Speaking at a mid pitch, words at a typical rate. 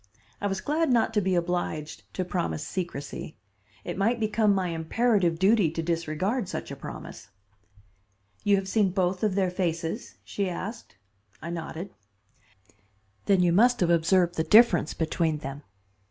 Yes: medium, 180 Hz; average, 155 wpm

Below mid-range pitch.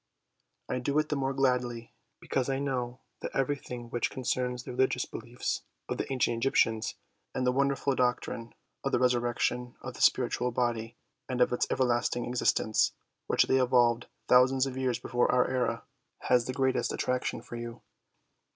Yes: low, 125 Hz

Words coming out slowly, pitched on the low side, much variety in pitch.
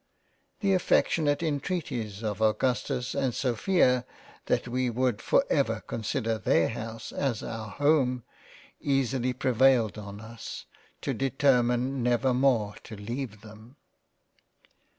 No: slow, 115 wpm; low, 125 Hz; average, 3.4 semitones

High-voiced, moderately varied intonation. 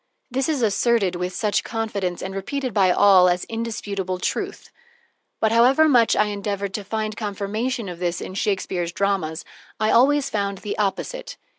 Yes: high, 205 Hz; average, 3.4 semitones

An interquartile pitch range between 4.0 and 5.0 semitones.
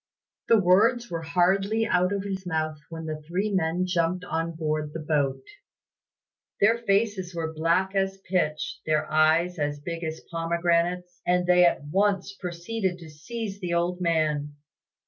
No: average, 3.1 semitones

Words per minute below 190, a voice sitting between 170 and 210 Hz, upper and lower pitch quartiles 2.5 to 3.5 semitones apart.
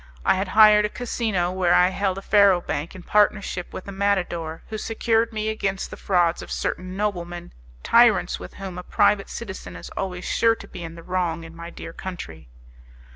No: average, 195 wpm; medium, 185 Hz; average, 3.1 semitones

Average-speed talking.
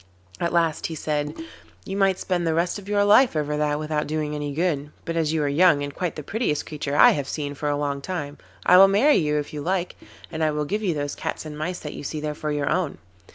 No: fast, 260 wpm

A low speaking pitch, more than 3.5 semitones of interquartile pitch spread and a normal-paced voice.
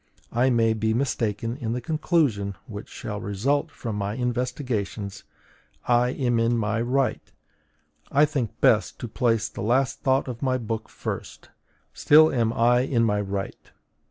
No: low, 120 Hz; average, 2.9 semitones; average, 155 wpm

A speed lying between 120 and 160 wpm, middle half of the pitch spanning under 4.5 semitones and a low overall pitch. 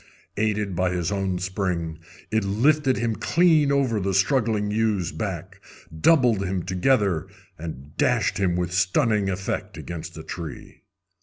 Yes: average, 140 wpm; average, 3.9 semitones; low, 100 Hz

